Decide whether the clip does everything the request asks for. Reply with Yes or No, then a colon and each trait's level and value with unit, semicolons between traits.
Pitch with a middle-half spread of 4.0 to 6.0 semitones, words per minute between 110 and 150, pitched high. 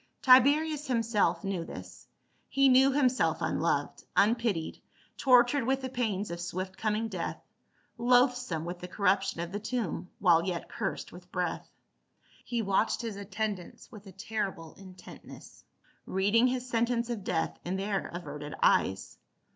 Yes: average, 5.1 semitones; average, 145 wpm; high, 210 Hz